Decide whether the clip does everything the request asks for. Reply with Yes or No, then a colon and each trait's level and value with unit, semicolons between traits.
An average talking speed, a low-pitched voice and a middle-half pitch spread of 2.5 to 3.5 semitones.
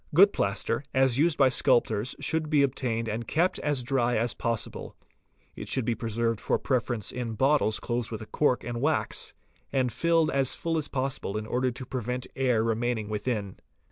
Yes: average, 180 wpm; low, 125 Hz; average, 3.1 semitones